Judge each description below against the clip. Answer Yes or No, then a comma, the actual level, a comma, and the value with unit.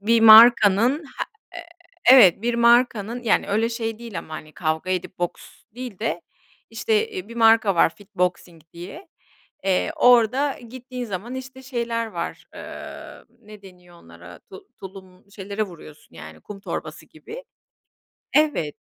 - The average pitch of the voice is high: Yes, high, 220 Hz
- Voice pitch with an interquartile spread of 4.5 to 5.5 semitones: Yes, average, 5.1 semitones